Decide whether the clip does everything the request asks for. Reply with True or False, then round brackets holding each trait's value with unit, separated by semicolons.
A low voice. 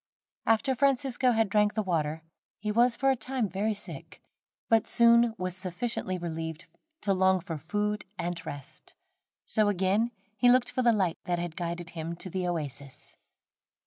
False (195 Hz)